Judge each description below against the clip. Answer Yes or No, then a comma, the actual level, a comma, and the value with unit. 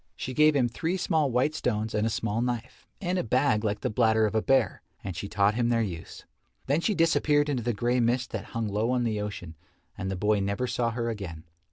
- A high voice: No, low, 115 Hz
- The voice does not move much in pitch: No, average, 3.5 semitones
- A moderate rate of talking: No, fast, 235 wpm